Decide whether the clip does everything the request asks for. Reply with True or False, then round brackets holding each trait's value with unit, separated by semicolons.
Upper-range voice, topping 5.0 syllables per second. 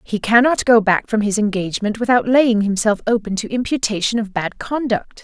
True (220 Hz; 5.3 syllables/s)